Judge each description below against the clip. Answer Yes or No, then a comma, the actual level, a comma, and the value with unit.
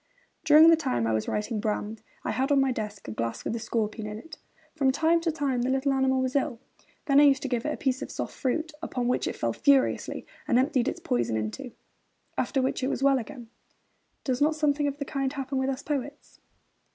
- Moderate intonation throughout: Yes, average, 3.6 semitones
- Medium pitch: No, very high, 265 Hz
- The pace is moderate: No, fast, 235 wpm